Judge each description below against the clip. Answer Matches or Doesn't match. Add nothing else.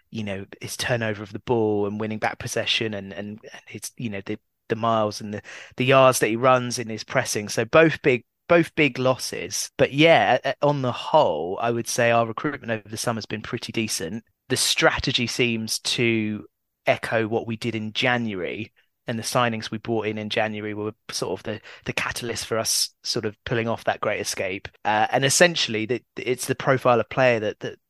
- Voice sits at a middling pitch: Doesn't match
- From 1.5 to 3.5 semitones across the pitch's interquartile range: Matches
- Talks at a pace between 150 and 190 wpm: Doesn't match